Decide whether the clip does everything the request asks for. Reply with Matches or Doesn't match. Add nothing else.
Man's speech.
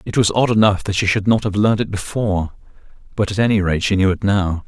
Matches